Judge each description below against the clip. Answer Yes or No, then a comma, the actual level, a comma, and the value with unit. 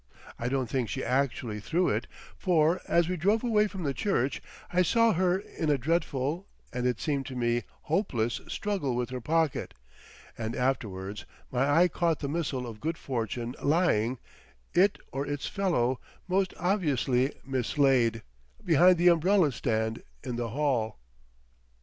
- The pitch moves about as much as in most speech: No, wide, 6.1 semitones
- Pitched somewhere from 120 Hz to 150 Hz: Yes, medium, 140 Hz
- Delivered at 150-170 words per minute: Yes, average, 155 wpm